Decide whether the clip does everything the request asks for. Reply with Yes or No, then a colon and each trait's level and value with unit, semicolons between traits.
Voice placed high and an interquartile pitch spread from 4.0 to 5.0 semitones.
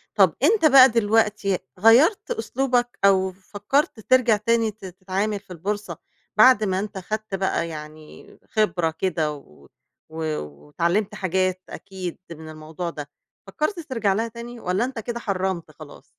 Yes: high, 200 Hz; average, 4.3 semitones